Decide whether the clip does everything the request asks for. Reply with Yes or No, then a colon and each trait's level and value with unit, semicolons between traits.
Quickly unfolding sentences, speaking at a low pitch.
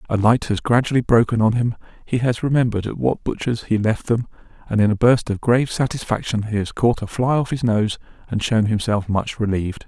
Yes: fast, 215 wpm; low, 115 Hz